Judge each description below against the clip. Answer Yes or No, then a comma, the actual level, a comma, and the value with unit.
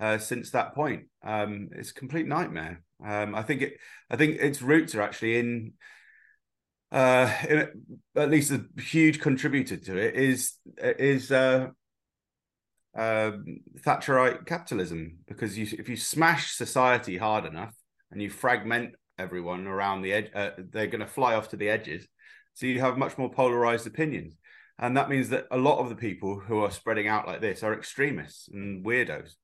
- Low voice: Yes, low, 120 Hz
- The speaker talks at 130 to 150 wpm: No, average, 175 wpm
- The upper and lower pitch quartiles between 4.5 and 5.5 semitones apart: Yes, average, 4.8 semitones